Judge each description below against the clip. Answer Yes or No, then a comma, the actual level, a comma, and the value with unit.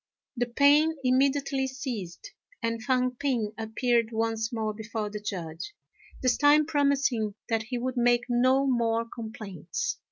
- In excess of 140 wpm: No, slow, 135 wpm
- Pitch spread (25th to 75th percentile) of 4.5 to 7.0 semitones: No, average, 3.3 semitones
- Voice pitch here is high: Yes, high, 240 Hz